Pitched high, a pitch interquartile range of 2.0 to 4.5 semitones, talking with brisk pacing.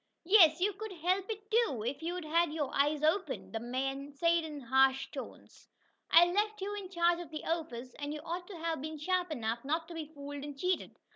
Yes: very high, 320 Hz; average, 4.1 semitones; fast, 215 wpm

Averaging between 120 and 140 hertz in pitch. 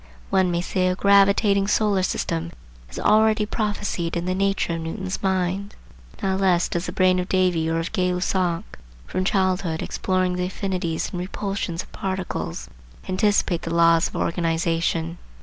No: medium, 185 Hz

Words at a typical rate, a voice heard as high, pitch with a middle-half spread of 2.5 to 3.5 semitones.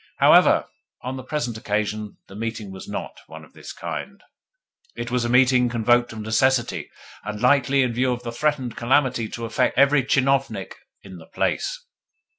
No: average, 170 wpm; low, 120 Hz; average, 3.1 semitones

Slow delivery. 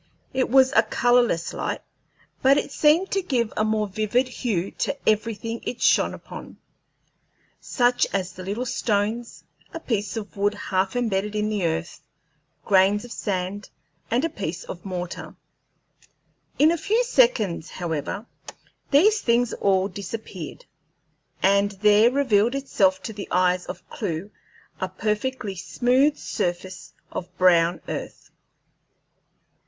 Yes: slow, 130 wpm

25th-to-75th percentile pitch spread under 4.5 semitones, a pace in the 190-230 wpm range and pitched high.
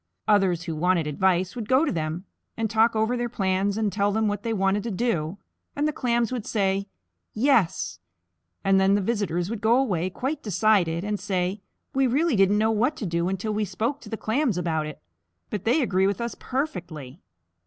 Yes: average, 4.0 semitones; average, 200 wpm; high, 205 Hz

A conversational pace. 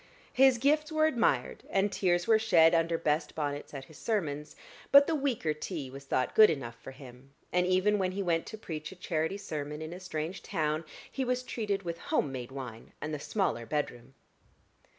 Yes: average, 195 wpm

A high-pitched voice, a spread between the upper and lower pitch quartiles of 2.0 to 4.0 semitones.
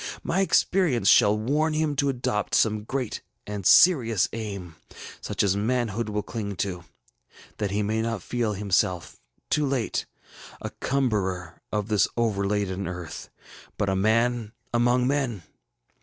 No: low, 110 Hz; average, 3.7 semitones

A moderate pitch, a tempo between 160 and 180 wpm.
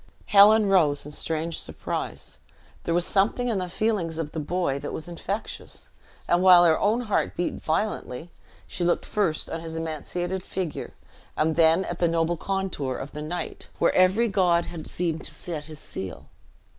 Yes: medium, 175 Hz; average, 175 wpm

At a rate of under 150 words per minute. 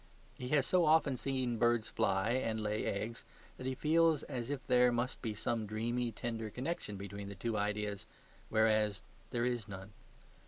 No: average, 170 wpm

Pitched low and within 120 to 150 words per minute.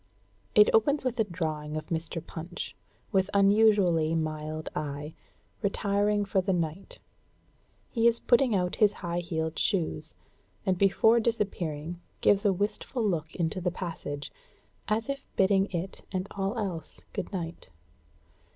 No: medium, 185 Hz; average, 140 wpm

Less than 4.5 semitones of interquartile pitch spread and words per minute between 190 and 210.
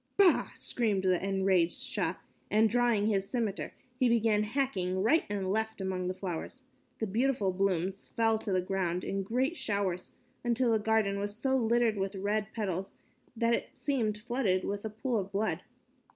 No: average, 3.4 semitones; average, 175 wpm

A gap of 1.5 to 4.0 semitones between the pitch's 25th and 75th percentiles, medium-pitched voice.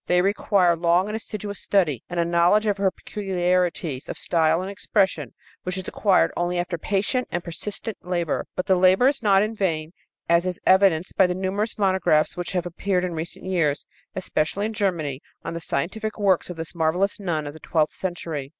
Yes: average, 2.7 semitones; medium, 180 Hz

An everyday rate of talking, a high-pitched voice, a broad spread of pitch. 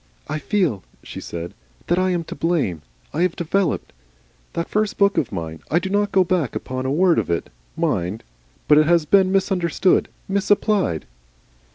No: average, 175 wpm; medium, 170 Hz; wide, 6.3 semitones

